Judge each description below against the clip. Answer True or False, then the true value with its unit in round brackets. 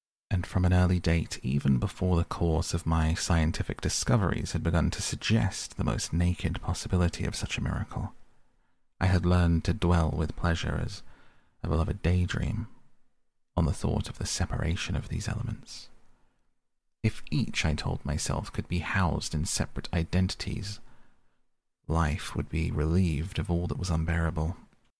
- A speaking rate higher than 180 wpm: False (165 wpm)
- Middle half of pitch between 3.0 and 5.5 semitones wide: False (2.4 semitones)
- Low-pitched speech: True (85 Hz)